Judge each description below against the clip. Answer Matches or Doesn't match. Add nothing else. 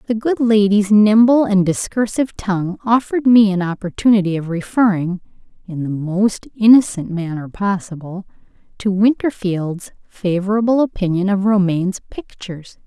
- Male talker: Doesn't match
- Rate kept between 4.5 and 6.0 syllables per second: Matches